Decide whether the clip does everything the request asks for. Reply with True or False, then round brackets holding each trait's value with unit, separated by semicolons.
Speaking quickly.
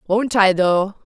False (160 wpm)